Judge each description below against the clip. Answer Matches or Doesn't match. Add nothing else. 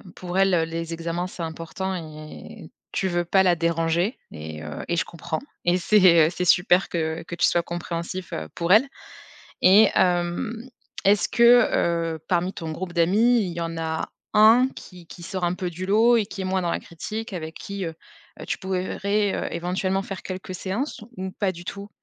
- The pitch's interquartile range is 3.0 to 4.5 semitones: Doesn't match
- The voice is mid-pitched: Matches